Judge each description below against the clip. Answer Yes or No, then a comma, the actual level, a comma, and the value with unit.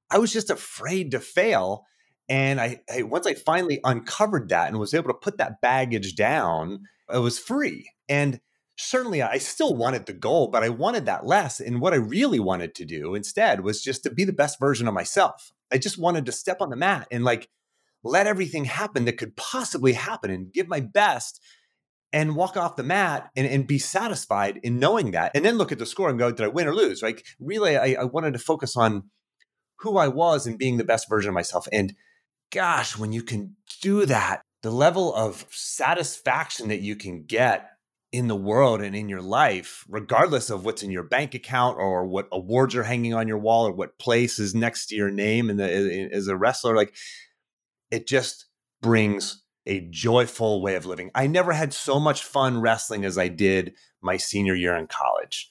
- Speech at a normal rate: No, fast, 210 wpm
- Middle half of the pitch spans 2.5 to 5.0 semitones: No, wide, 5.4 semitones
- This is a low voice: Yes, low, 120 Hz